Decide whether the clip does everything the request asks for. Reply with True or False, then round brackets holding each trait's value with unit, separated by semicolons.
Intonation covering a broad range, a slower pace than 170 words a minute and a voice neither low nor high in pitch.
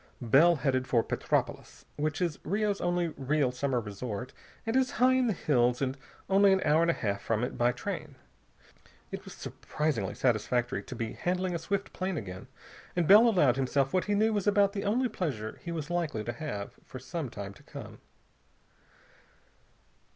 False (7.4 semitones; 180 wpm; 150 Hz)